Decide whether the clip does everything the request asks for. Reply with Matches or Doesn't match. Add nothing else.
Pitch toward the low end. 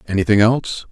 Matches